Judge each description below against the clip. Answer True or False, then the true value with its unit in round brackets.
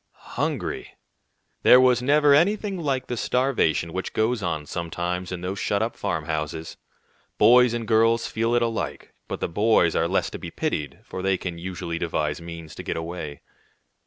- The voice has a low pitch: True (95 Hz)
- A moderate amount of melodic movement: False (6.1 semitones)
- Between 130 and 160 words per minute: False (170 wpm)